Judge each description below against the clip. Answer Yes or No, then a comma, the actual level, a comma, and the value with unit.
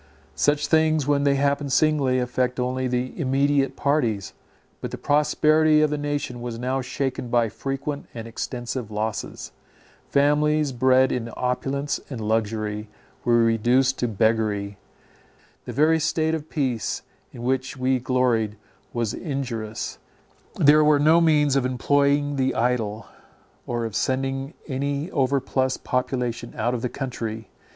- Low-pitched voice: Yes, low, 130 Hz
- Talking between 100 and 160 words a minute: Yes, average, 140 wpm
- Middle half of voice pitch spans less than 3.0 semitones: No, average, 3.3 semitones